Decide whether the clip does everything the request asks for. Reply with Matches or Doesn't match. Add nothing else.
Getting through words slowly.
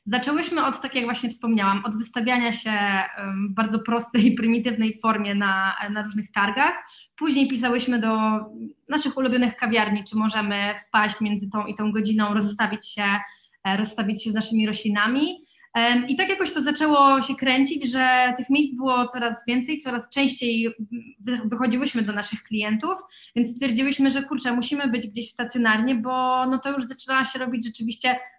Doesn't match